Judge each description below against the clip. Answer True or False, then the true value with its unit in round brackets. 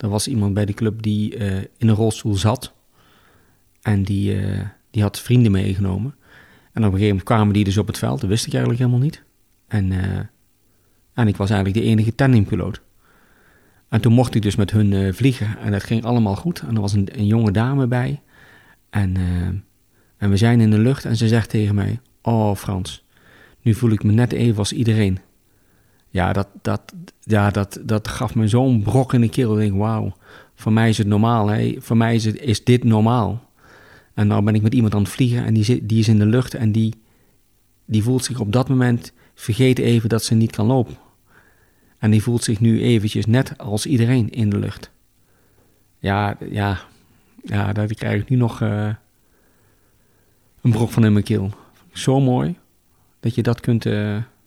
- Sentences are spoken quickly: True (205 wpm)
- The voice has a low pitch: True (110 Hz)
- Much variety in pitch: False (2.6 semitones)